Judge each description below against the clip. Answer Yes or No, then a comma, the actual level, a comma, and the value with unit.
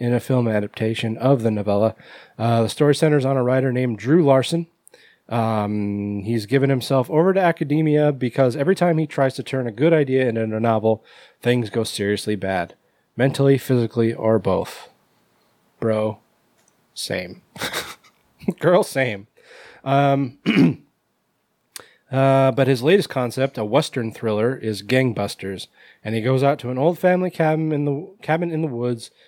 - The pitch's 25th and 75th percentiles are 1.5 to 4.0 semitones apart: No, average, 4.4 semitones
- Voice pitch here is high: No, low, 130 Hz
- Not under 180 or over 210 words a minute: No, average, 155 wpm